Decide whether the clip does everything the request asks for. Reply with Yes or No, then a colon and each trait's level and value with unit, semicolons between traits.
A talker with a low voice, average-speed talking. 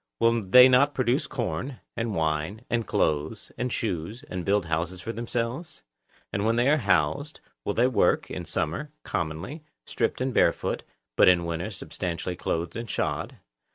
Yes: low, 115 Hz; average, 160 wpm